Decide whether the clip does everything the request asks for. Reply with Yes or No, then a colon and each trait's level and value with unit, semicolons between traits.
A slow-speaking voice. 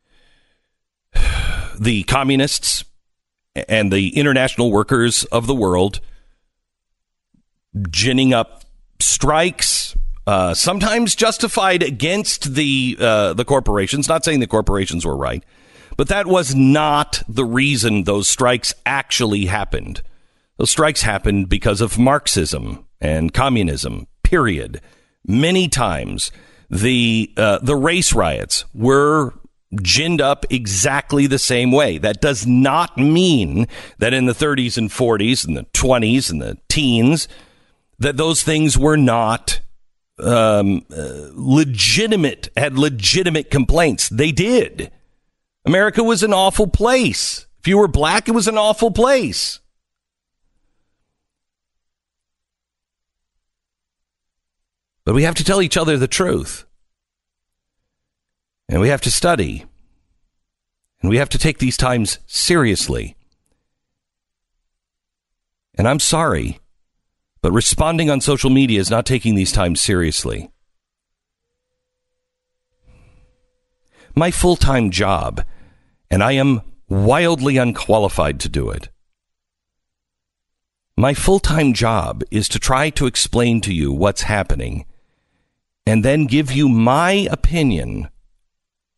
Yes: slow, 115 wpm